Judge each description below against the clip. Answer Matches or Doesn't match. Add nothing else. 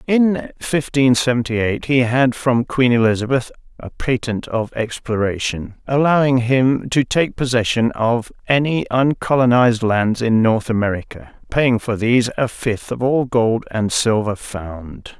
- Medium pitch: Doesn't match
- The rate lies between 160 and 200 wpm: Doesn't match